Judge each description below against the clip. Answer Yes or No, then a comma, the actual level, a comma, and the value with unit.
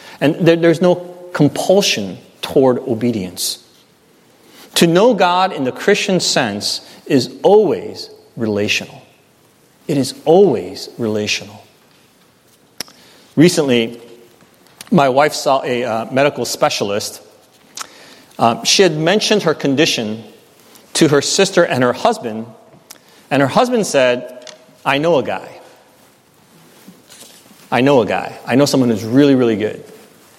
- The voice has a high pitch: No, medium, 140 Hz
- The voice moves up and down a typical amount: No, wide, 7.0 semitones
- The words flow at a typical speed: No, slow, 115 wpm